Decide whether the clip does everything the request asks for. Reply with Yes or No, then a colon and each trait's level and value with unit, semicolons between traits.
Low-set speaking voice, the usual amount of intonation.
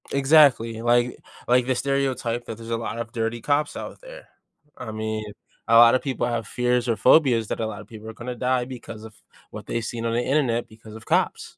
No: low, 120 Hz; narrow, 2.1 semitones